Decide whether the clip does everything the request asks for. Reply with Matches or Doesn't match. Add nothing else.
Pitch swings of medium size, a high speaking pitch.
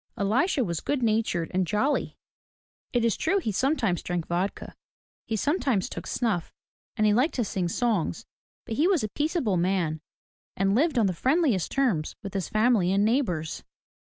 Doesn't match